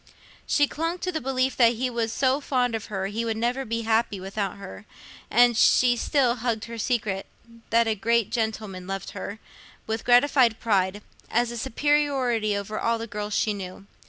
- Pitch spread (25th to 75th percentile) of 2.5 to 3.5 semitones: Yes, average, 2.9 semitones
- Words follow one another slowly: No, average, 175 wpm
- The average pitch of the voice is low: No, high, 230 Hz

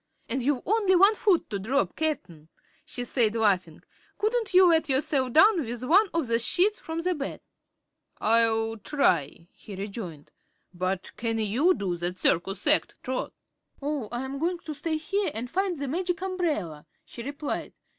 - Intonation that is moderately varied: No, wide, 7.7 semitones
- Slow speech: No, average, 165 wpm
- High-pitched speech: Yes, very high, 265 Hz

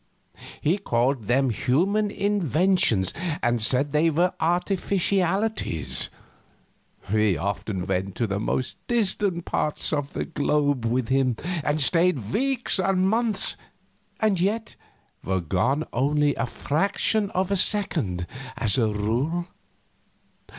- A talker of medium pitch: Yes, medium, 150 Hz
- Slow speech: Yes, slow, 120 wpm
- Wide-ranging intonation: Yes, wide, 8.5 semitones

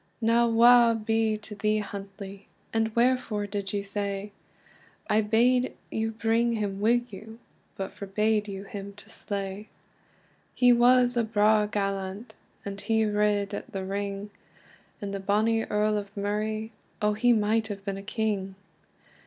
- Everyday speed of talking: Yes, average, 150 wpm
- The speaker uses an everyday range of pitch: No, narrow, 1.9 semitones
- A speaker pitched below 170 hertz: No, high, 210 Hz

